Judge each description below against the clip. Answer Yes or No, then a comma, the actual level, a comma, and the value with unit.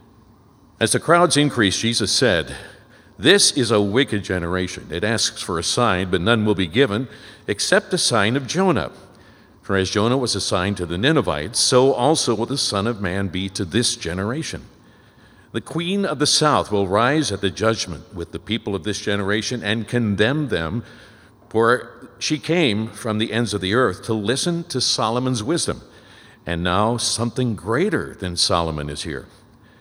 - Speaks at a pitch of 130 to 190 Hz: No, low, 110 Hz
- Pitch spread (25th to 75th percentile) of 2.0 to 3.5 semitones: No, average, 4.0 semitones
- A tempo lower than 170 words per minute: No, average, 175 wpm